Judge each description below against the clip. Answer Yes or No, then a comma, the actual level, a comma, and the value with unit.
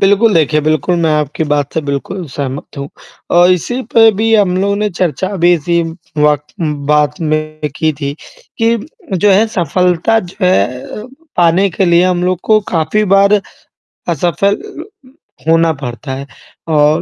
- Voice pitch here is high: No, medium, 170 Hz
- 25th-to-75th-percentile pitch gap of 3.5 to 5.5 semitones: Yes, average, 4.5 semitones